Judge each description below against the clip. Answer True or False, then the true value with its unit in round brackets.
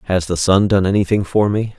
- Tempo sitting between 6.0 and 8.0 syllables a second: False (5.7 syllables/s)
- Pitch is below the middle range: True (100 Hz)